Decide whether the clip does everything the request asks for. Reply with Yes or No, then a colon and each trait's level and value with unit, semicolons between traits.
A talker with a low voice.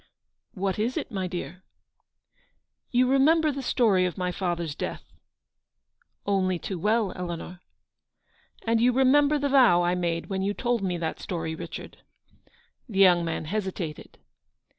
No: high, 190 Hz